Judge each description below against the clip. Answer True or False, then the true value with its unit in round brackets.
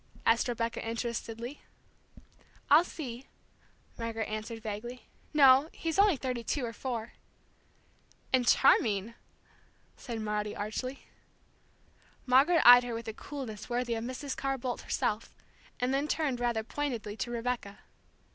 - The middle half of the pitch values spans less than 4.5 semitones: True (2.8 semitones)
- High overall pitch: True (240 Hz)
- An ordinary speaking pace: False (130 wpm)